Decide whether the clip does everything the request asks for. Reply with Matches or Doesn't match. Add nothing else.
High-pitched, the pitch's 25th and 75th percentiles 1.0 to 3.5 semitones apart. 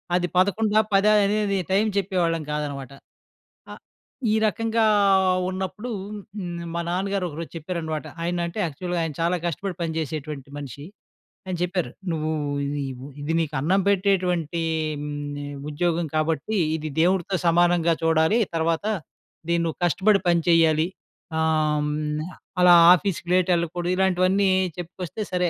Doesn't match